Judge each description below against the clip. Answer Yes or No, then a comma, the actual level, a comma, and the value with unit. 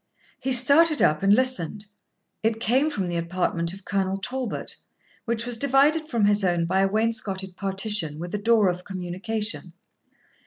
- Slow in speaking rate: No, average, 160 wpm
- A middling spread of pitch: Yes, average, 4.2 semitones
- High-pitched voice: Yes, high, 205 Hz